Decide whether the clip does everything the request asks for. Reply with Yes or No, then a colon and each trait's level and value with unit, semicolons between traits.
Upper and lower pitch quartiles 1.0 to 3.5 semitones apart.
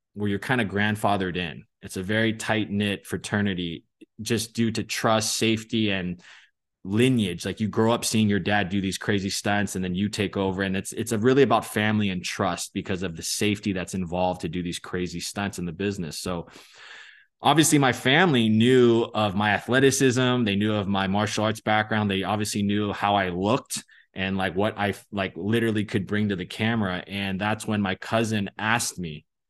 Yes: narrow, 2.5 semitones